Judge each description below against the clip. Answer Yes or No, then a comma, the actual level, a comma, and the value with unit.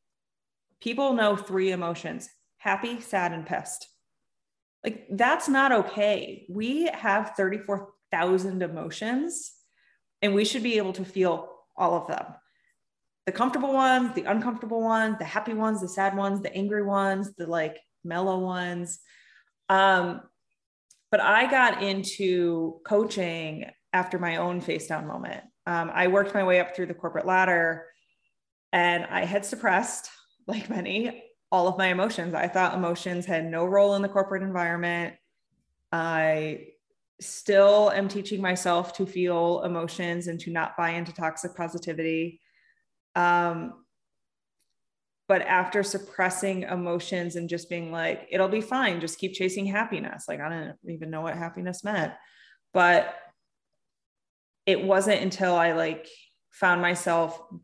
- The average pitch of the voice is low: No, medium, 185 Hz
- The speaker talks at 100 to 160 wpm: Yes, average, 140 wpm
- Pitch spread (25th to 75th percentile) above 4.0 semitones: No, average, 3.0 semitones